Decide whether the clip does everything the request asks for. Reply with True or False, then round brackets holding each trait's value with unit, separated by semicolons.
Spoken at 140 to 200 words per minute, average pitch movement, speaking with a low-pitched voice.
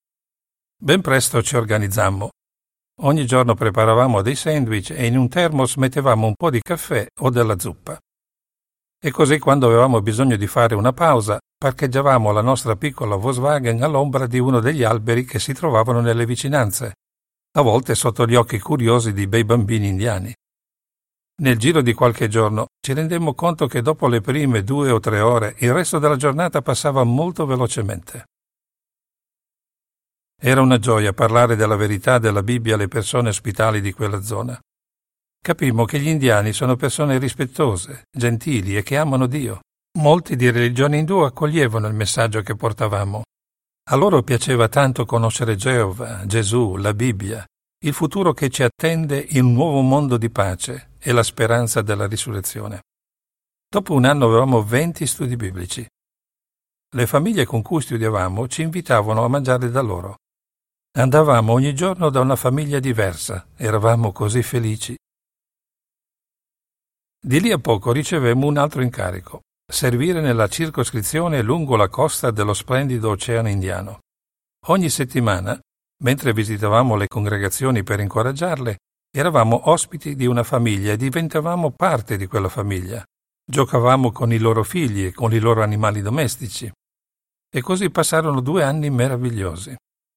True (145 wpm; 4.1 semitones; 120 Hz)